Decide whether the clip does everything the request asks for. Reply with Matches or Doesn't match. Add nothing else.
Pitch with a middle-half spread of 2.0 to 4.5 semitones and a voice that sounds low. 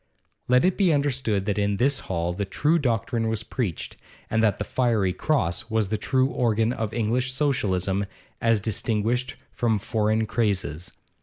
Matches